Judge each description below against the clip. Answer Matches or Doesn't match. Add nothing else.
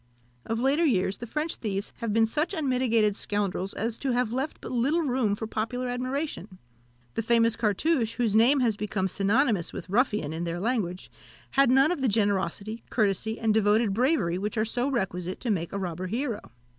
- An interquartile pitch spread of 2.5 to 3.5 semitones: Doesn't match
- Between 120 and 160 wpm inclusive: Doesn't match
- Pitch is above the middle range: Matches